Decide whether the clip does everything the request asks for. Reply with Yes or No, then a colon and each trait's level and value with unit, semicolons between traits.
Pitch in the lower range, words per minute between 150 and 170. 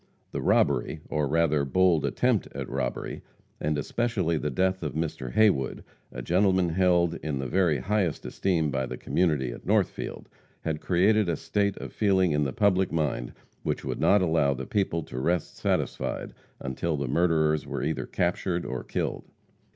Yes: very low, 80 Hz; average, 165 wpm